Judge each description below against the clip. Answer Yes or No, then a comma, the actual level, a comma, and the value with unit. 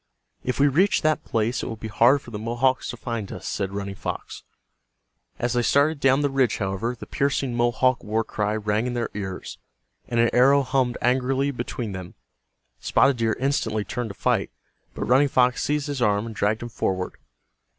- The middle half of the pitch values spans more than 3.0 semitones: Yes, average, 3.6 semitones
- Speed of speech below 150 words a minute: No, average, 190 wpm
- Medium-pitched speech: No, low, 120 Hz